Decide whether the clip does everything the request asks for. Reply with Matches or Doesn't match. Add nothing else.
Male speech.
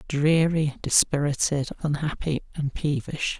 Matches